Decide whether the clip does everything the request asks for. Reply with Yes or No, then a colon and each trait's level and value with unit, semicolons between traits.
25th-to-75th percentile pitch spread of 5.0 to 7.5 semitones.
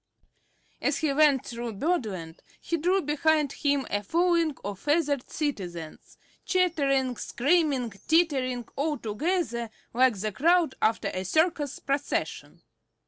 Yes: wide, 5.4 semitones